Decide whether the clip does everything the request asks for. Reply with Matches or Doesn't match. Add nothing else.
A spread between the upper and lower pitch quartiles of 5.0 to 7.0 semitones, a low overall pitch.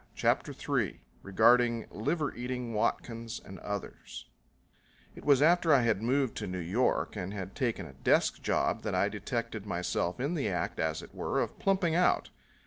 Matches